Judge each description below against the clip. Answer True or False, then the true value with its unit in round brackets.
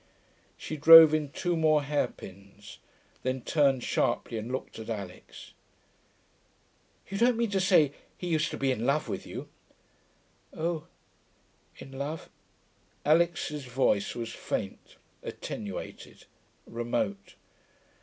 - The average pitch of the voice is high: False (140 Hz)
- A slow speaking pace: True (115 wpm)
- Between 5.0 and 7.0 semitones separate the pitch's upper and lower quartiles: True (5.6 semitones)